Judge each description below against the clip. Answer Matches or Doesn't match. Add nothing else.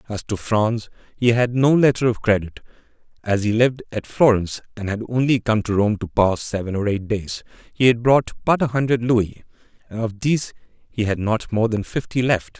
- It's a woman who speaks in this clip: Doesn't match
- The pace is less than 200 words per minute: Doesn't match